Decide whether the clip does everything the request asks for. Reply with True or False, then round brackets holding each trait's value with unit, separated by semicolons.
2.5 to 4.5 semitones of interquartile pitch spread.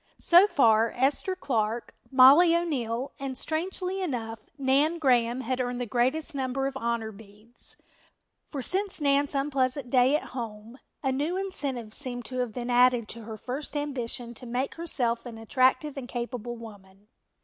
True (3.4 semitones)